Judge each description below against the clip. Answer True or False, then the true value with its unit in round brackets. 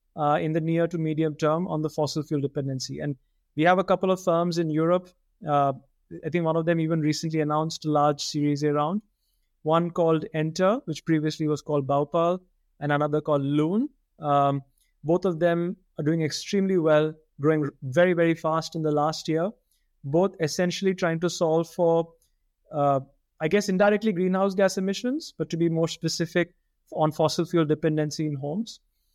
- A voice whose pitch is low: False (160 Hz)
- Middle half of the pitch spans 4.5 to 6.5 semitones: False (2.6 semitones)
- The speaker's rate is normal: True (175 wpm)